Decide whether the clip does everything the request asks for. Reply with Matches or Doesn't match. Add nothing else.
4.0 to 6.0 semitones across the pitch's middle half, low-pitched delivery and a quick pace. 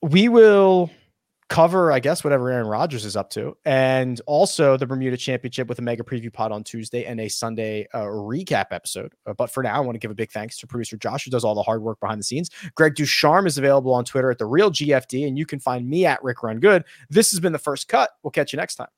Matches